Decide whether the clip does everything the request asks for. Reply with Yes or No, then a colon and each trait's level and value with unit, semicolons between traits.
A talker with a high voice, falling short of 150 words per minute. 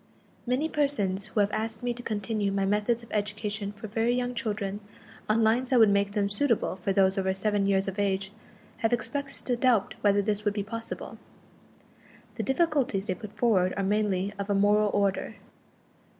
No: high, 210 Hz; average, 185 wpm